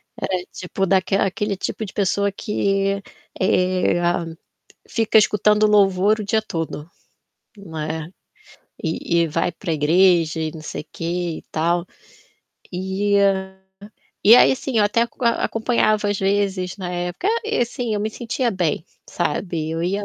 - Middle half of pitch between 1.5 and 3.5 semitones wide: Yes, average, 3.2 semitones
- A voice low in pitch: No, high, 195 Hz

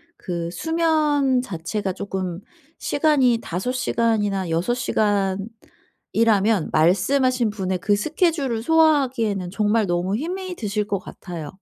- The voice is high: Yes, high, 215 Hz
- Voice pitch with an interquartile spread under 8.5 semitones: Yes, wide, 5.6 semitones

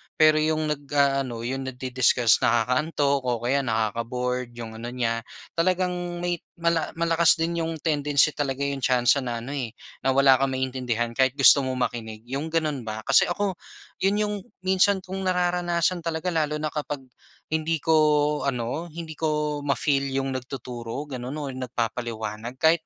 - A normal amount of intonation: Yes, average, 4.5 semitones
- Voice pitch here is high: No, medium, 140 Hz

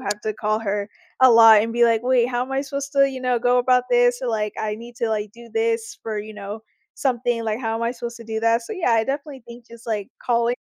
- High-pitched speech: Yes, high, 235 Hz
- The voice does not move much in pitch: Yes, narrow, 2.0 semitones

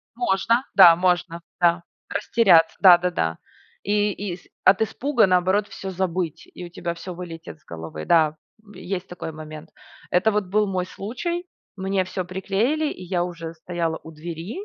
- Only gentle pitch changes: No, average, 3.0 semitones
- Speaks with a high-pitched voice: No, medium, 180 Hz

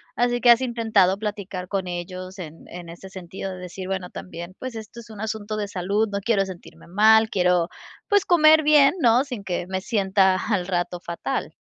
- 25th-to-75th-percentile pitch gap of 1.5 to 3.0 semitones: No, average, 3.7 semitones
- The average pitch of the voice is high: Yes, high, 195 Hz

